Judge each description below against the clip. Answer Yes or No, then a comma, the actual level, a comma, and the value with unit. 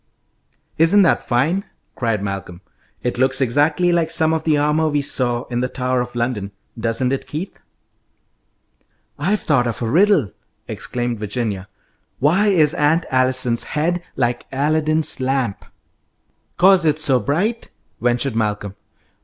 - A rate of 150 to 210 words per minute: No, slow, 135 wpm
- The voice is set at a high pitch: No, low, 135 Hz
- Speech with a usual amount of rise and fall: Yes, average, 4.9 semitones